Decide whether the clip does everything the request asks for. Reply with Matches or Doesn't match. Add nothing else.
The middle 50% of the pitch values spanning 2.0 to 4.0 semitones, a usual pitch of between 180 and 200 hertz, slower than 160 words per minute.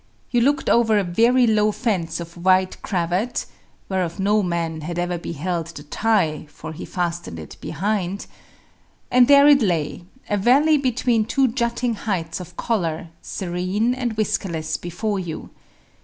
Doesn't match